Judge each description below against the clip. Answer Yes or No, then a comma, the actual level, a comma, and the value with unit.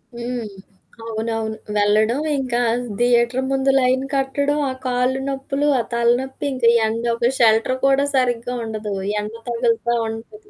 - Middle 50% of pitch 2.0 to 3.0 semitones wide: Yes, average, 2.7 semitones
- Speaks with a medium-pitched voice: No, high, 245 Hz